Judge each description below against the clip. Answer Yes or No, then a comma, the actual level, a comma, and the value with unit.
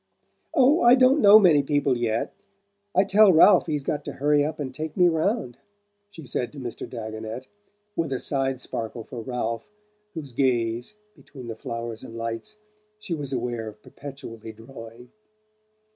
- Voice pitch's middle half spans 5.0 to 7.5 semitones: Yes, wide, 5.6 semitones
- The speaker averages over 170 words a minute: No, average, 160 wpm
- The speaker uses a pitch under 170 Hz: Yes, low, 135 Hz